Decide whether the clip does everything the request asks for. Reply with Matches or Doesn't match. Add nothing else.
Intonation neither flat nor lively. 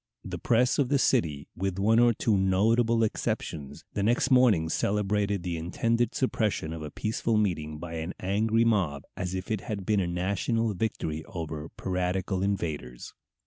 Matches